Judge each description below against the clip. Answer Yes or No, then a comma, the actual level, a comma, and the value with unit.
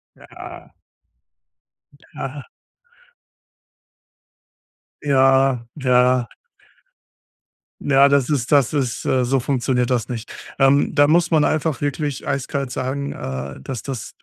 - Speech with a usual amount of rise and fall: No, narrow, 2.2 semitones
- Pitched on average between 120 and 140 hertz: Yes, low, 135 Hz